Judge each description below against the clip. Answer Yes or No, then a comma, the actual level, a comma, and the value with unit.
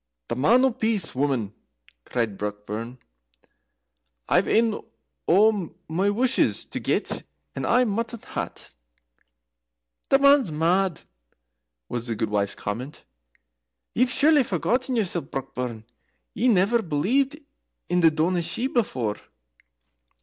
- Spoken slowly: Yes, slow, 115 wpm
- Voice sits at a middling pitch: Yes, medium, 180 Hz